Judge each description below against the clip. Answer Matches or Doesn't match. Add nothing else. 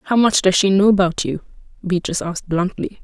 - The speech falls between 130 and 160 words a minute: Doesn't match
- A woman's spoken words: Matches